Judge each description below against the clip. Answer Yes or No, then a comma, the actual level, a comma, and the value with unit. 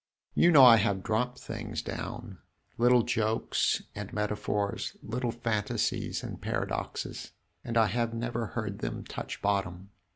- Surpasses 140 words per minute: No, slow, 135 wpm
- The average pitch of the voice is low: Yes, low, 115 Hz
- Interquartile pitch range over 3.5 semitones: No, narrow, 2.5 semitones